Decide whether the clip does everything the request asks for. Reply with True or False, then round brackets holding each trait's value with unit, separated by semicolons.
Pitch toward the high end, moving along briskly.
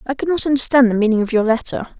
True (245 Hz; 270 wpm)